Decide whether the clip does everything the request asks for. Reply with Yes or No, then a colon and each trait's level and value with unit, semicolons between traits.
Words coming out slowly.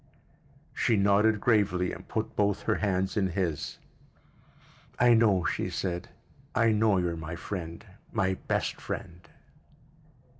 Yes: slow, 125 wpm